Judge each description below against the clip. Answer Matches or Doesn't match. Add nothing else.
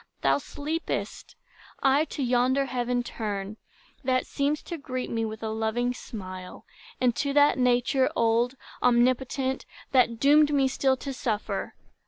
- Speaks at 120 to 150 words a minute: Matches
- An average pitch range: Matches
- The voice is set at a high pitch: Matches